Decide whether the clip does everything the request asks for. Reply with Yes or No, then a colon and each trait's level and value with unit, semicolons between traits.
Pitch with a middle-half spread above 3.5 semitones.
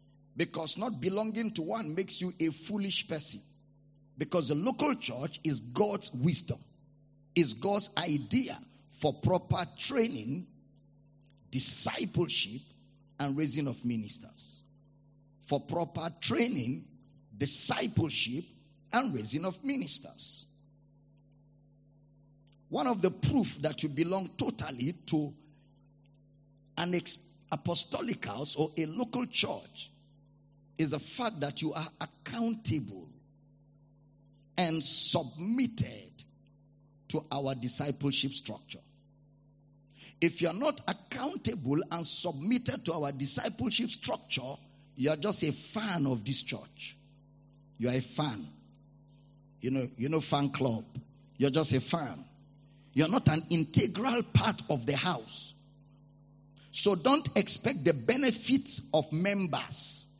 No: average, 2.8 semitones